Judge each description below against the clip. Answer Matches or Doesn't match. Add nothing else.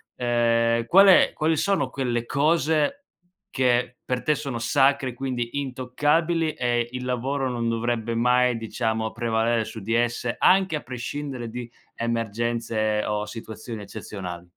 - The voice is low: Matches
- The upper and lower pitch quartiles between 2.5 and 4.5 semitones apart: Matches